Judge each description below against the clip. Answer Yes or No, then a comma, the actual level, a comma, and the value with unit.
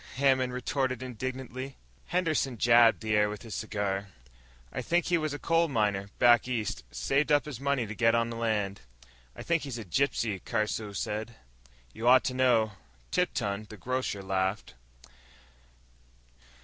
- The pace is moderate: Yes, average, 155 wpm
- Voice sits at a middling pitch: No, low, 120 Hz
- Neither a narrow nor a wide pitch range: Yes, average, 3.8 semitones